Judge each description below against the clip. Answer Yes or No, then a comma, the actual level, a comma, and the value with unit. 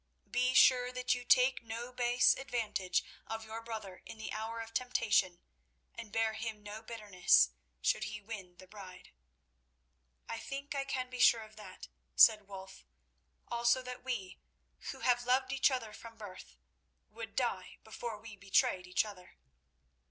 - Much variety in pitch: No, average, 3.2 semitones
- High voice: Yes, high, 225 Hz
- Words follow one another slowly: No, average, 160 wpm